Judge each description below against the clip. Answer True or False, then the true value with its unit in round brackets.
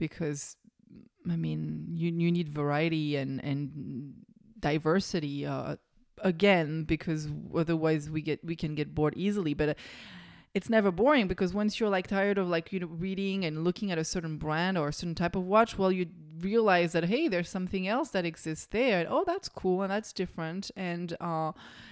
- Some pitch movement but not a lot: True (4.0 semitones)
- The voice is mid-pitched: True (175 Hz)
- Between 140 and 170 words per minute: False (185 wpm)